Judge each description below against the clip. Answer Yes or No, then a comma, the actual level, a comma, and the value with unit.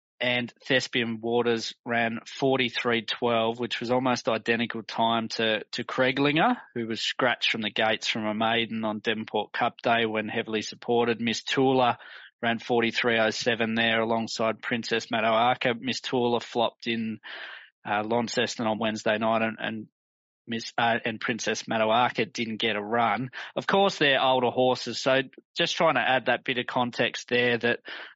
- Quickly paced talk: No, average, 155 wpm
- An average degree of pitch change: No, narrow, 1.7 semitones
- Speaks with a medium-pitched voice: No, low, 115 Hz